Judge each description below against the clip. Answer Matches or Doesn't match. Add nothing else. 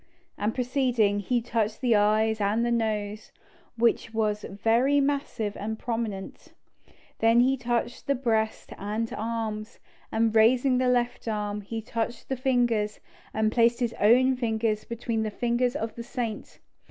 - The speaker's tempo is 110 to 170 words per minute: Matches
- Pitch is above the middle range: Matches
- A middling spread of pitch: Doesn't match